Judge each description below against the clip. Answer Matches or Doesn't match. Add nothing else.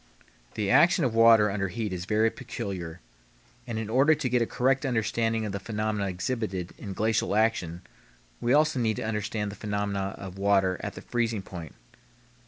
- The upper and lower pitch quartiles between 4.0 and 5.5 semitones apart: Doesn't match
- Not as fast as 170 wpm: Doesn't match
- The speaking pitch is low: Matches